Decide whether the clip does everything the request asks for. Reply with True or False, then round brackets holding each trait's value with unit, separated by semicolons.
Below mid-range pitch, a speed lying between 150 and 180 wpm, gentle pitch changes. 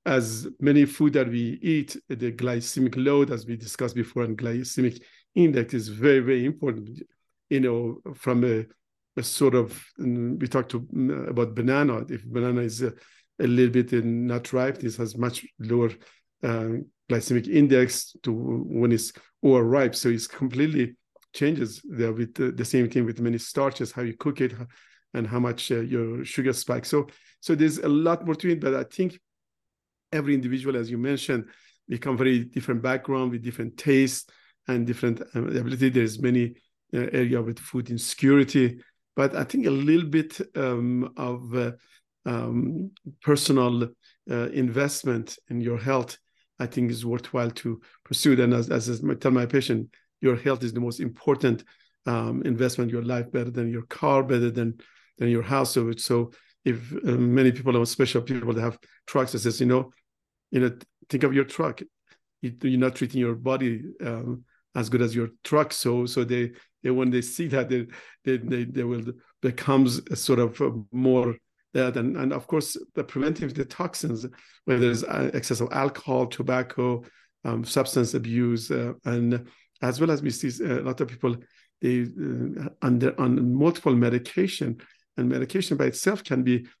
True (125 Hz; 170 wpm; 2.1 semitones)